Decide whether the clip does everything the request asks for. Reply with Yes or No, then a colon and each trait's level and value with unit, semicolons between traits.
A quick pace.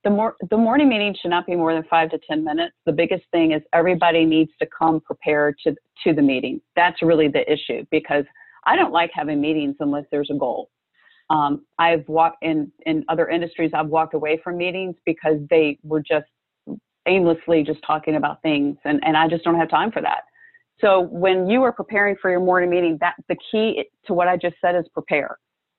Yes: fast, 210 wpm